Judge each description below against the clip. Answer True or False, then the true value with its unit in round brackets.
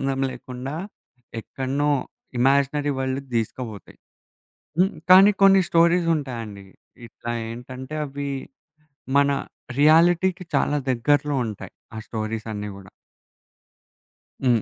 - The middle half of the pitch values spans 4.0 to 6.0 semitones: True (4.4 semitones)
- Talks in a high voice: False (135 Hz)